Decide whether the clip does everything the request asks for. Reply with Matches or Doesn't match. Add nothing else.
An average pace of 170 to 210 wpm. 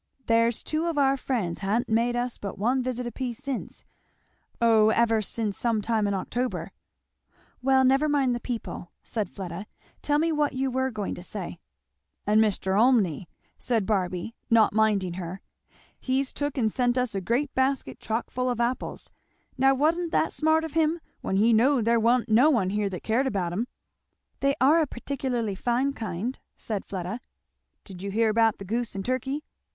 Matches